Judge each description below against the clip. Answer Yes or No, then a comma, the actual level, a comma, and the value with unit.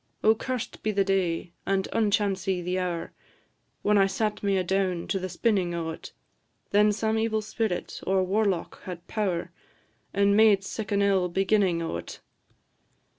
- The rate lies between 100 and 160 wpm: Yes, average, 150 wpm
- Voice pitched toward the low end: No, high, 195 Hz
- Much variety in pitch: No, narrow, 2.5 semitones